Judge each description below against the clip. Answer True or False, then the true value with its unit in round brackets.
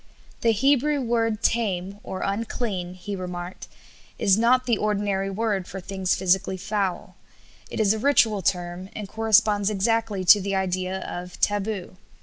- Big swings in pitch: False (3.0 semitones)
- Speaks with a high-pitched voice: True (200 Hz)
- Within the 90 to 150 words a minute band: True (140 wpm)